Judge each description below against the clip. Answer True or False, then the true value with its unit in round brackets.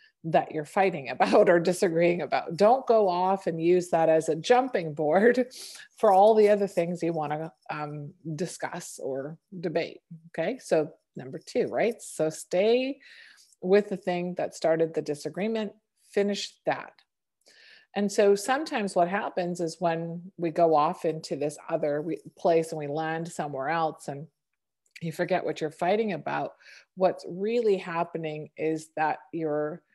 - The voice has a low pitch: False (175 Hz)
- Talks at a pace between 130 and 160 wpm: True (155 wpm)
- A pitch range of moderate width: True (4.1 semitones)